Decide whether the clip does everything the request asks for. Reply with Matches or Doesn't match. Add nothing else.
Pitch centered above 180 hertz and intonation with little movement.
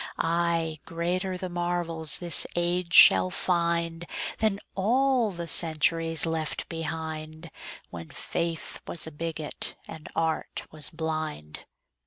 Doesn't match